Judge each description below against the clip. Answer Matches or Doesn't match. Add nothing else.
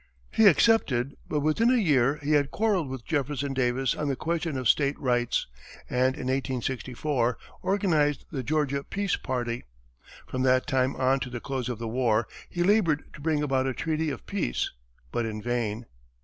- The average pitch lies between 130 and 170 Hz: Matches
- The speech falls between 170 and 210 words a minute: Matches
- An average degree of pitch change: Matches